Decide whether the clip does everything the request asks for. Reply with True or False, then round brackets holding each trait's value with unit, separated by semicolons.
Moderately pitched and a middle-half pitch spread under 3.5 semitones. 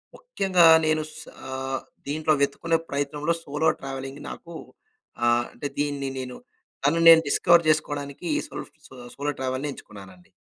True (145 Hz; 3.0 semitones)